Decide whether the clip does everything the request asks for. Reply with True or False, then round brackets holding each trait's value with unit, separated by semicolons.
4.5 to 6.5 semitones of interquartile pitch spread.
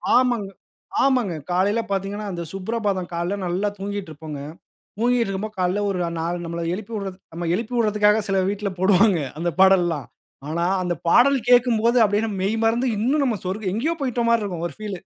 False (3.9 semitones)